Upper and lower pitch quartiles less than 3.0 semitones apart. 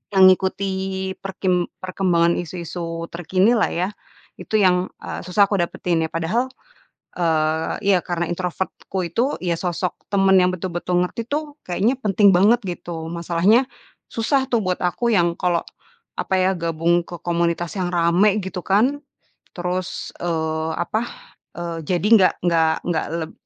Yes: narrow, 2.4 semitones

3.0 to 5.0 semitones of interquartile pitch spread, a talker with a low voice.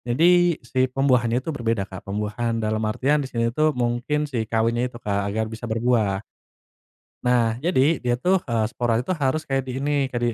Yes: average, 3.4 semitones; low, 120 Hz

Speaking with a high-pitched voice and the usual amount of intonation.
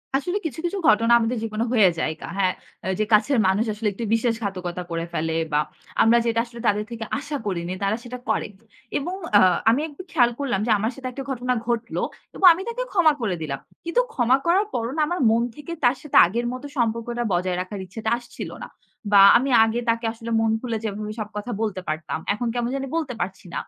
Yes: high, 230 Hz; average, 3.7 semitones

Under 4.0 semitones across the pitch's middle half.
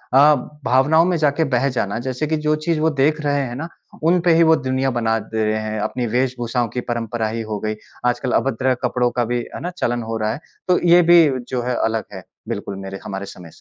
No: average, 5.2 semitones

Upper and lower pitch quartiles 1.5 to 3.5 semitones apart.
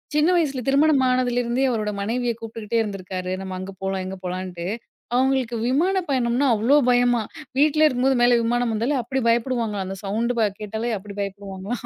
No: average, 4.2 semitones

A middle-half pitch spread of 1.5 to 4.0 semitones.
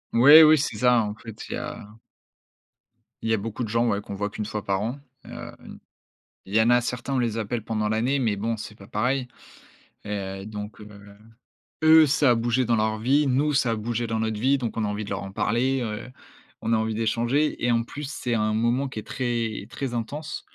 Yes: average, 2.8 semitones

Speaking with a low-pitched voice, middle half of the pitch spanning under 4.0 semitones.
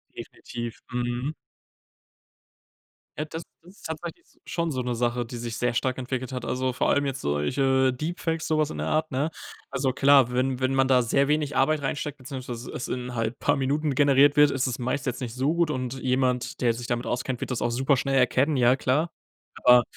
Yes: low, 130 Hz; narrow, 2.6 semitones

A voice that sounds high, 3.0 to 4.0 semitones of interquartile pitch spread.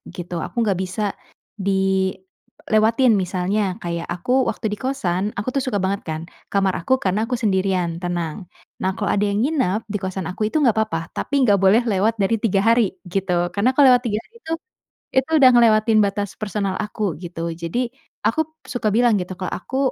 Yes: high, 200 Hz; average, 3.5 semitones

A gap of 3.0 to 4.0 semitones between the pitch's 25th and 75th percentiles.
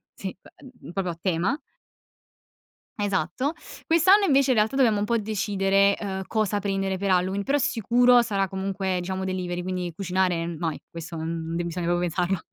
Yes: average, 3.4 semitones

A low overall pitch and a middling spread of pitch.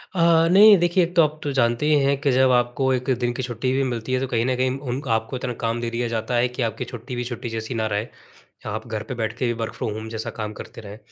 Yes: low, 125 Hz; average, 3.0 semitones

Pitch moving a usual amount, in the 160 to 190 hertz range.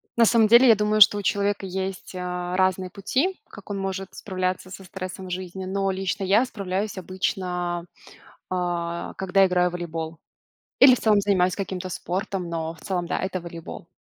No: narrow, 1.9 semitones; medium, 185 Hz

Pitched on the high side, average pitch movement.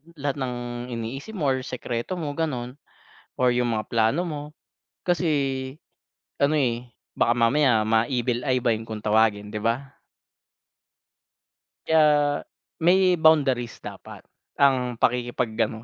No: low, 125 Hz; average, 4.0 semitones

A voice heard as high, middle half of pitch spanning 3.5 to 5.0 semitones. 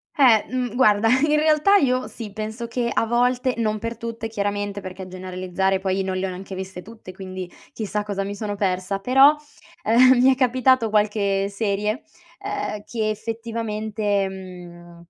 Yes: high, 215 Hz; average, 3.8 semitones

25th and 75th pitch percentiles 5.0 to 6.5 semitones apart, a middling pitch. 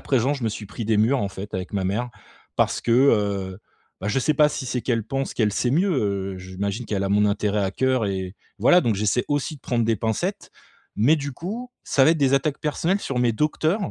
No: average, 5.3 semitones; low, 120 Hz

